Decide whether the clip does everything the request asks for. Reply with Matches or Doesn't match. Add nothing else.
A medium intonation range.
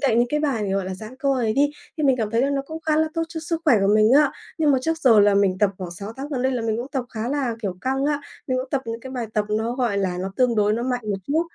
Matches